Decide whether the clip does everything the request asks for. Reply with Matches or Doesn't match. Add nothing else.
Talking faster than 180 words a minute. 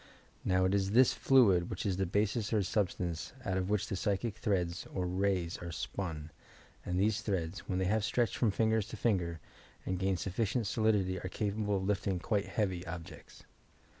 Matches